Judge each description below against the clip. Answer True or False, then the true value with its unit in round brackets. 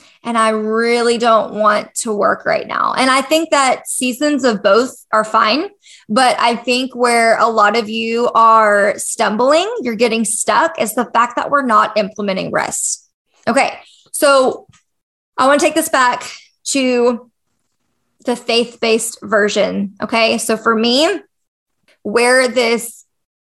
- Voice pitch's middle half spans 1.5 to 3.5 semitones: True (2.8 semitones)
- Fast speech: False (150 wpm)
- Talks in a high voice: True (235 Hz)